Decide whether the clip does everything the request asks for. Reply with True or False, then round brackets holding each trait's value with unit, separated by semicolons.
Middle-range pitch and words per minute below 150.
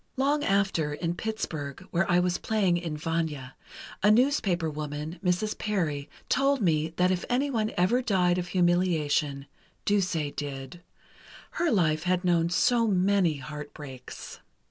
True (175 Hz; 135 wpm)